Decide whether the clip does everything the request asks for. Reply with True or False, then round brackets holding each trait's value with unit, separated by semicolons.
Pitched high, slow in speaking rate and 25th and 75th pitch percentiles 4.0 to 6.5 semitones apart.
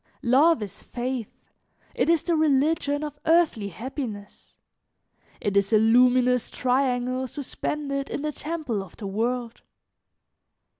True (255 Hz; 120 wpm; 4.4 semitones)